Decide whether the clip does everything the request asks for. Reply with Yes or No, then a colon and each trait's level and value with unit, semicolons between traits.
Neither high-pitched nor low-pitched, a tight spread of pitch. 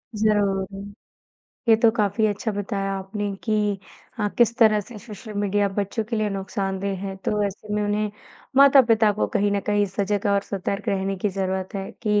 No: high, 205 Hz; narrow, 1.5 semitones